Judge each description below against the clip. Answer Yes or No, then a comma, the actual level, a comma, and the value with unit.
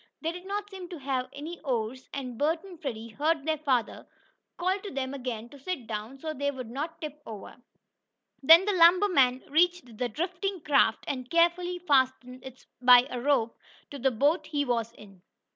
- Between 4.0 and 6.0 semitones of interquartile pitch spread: Yes, average, 5.2 semitones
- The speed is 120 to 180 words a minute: No, average, 190 wpm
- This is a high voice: Yes, very high, 280 Hz